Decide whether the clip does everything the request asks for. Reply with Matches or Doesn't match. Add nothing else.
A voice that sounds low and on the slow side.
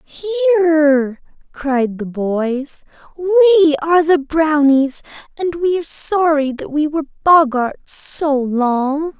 Doesn't match